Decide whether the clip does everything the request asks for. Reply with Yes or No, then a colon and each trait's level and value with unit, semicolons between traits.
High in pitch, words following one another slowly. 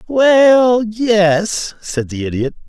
Yes: high, 200 Hz; slow, 90 wpm